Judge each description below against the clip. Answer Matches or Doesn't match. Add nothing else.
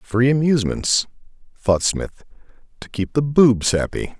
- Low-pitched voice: Matches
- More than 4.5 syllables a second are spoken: Doesn't match